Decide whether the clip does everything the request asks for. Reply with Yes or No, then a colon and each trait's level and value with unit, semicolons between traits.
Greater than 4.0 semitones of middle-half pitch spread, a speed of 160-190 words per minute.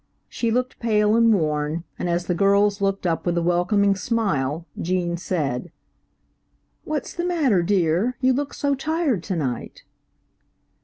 No: average, 5.3 semitones; average, 150 wpm